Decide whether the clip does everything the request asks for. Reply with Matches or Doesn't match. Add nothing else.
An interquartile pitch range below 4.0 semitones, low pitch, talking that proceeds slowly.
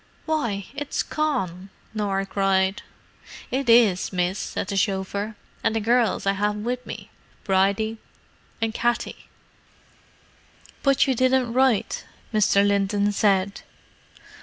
Doesn't match